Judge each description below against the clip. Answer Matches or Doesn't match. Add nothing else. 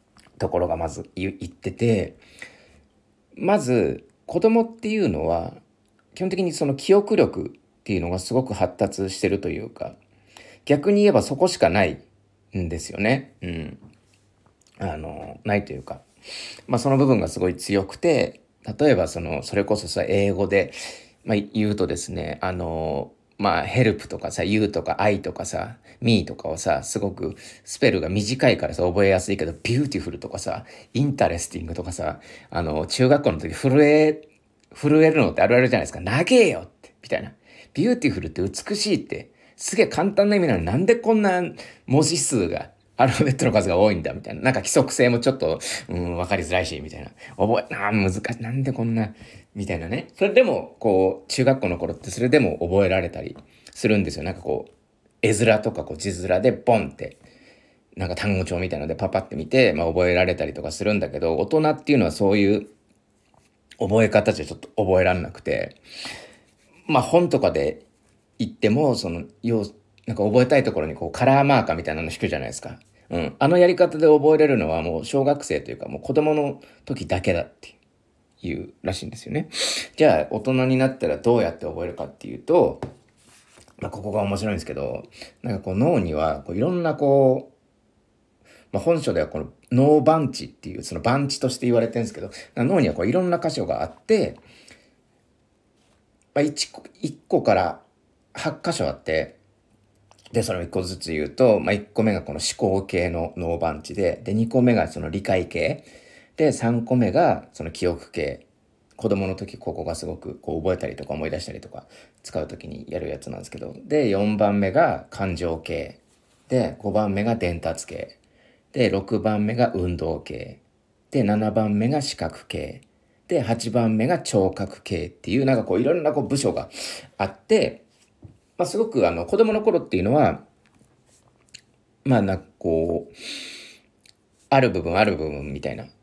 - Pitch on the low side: Matches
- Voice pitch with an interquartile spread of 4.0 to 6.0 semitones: Doesn't match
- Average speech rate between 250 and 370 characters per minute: Matches